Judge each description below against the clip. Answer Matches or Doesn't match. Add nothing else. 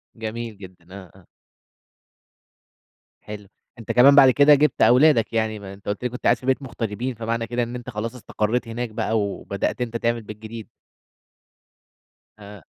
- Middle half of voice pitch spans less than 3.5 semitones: Matches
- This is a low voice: Matches